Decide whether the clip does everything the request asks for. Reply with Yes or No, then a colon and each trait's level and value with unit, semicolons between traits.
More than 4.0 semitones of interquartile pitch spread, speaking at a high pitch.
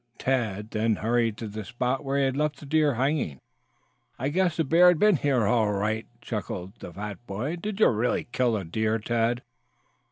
No: average, 5.0 semitones; low, 120 Hz